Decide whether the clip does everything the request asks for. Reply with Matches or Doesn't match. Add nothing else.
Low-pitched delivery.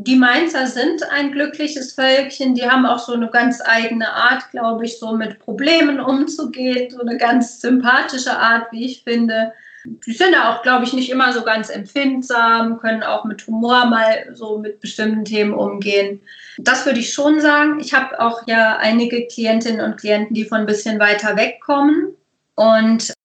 Doesn't match